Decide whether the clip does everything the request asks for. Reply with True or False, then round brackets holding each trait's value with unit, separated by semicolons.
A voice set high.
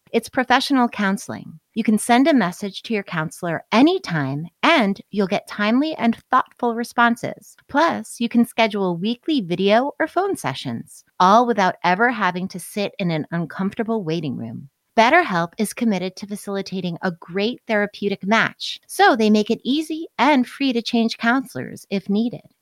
True (220 Hz)